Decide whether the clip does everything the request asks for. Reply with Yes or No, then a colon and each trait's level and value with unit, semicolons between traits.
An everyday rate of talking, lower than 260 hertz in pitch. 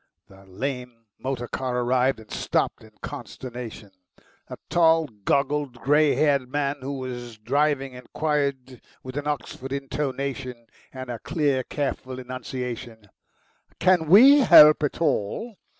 No: slow, 125 wpm; low, 135 Hz